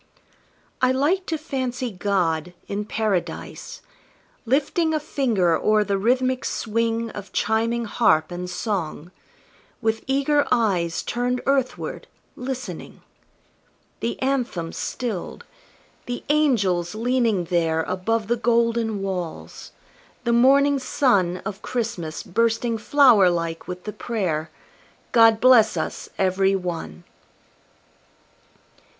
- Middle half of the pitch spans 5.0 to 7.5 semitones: Yes, wide, 5.4 semitones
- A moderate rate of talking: No, slow, 110 wpm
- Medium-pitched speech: No, high, 225 Hz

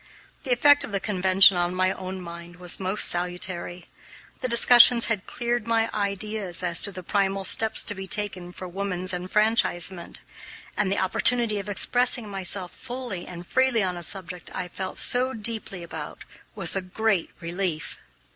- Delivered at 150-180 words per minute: Yes, average, 165 wpm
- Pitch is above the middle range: Yes, high, 195 Hz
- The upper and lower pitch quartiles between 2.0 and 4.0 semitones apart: Yes, average, 3.6 semitones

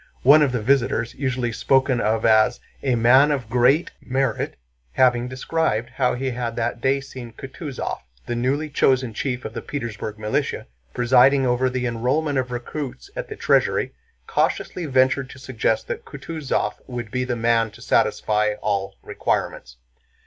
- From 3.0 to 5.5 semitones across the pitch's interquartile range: No, narrow, 2.5 semitones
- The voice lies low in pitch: Yes, low, 125 Hz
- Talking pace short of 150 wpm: No, average, 155 wpm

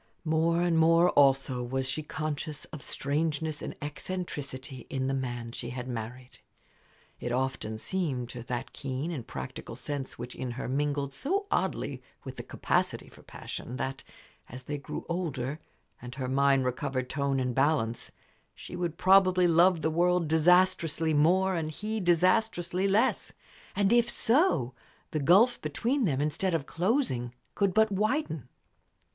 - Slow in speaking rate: No, average, 150 wpm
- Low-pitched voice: No, medium, 150 Hz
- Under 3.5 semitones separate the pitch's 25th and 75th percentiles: No, average, 5.3 semitones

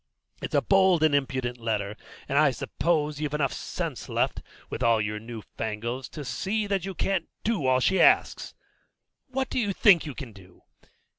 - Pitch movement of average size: No, wide, 8.2 semitones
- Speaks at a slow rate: No, average, 180 wpm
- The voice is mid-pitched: Yes, medium, 145 Hz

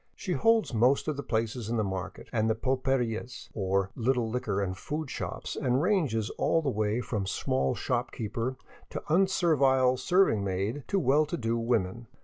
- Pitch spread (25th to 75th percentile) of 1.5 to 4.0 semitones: No, average, 4.4 semitones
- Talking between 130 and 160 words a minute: No, average, 175 wpm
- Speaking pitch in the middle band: No, low, 120 Hz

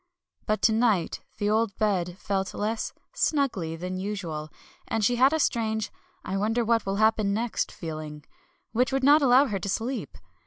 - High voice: Yes, high, 215 Hz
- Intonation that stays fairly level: No, average, 3.8 semitones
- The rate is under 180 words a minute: Yes, average, 170 wpm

